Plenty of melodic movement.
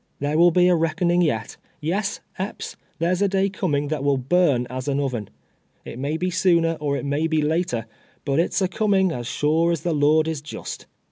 No: average, 3.8 semitones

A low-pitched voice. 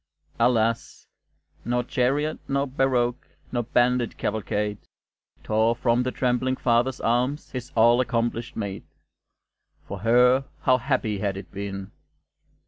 Yes: low, 120 Hz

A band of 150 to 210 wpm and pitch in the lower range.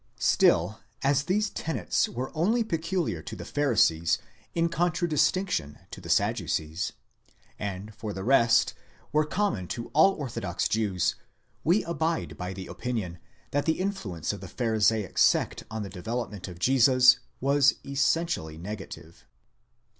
No: average, 140 wpm; low, 125 Hz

